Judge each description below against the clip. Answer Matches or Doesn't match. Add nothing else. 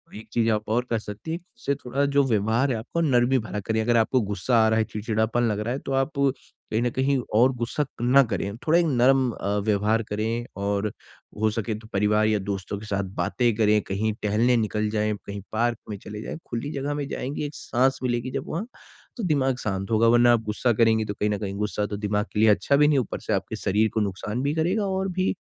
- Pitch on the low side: Matches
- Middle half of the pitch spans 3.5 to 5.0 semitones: Matches